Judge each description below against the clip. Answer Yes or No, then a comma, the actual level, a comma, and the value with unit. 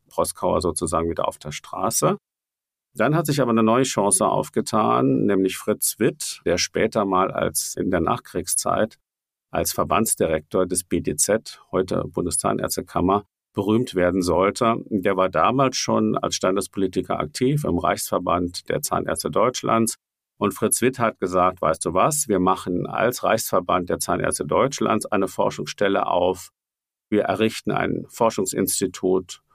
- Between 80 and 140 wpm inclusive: Yes, average, 135 wpm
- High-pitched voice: No, low, 100 Hz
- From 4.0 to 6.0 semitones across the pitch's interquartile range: No, average, 3.5 semitones